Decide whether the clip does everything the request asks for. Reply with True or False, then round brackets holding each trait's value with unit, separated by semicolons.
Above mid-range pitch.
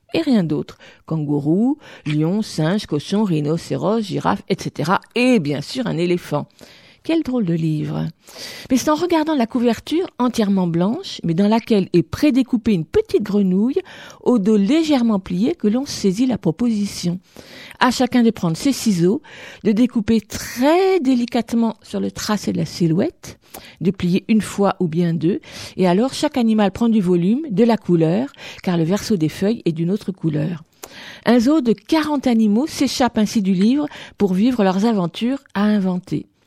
True (215 Hz)